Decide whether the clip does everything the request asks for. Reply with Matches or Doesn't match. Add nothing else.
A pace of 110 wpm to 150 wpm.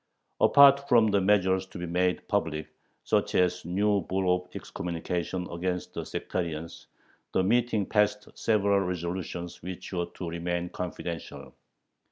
Matches